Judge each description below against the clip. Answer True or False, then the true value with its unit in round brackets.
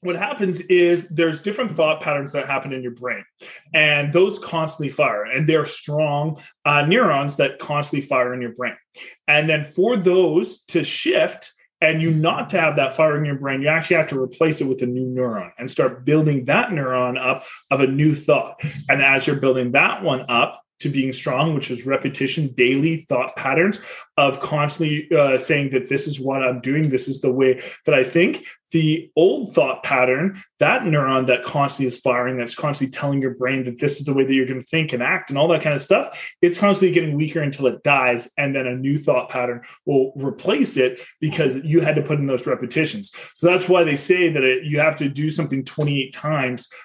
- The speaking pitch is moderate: True (145 Hz)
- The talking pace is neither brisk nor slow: False (215 wpm)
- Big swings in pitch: False (3.5 semitones)